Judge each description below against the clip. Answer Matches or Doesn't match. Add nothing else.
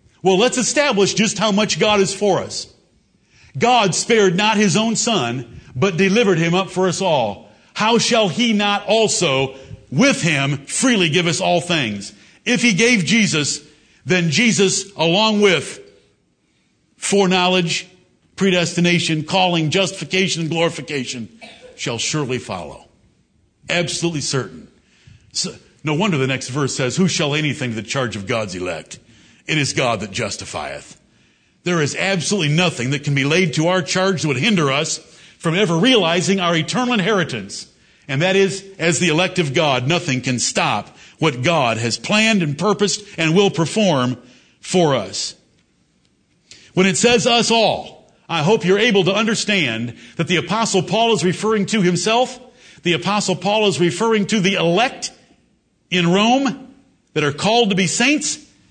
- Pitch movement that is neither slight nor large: Doesn't match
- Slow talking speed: Doesn't match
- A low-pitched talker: Doesn't match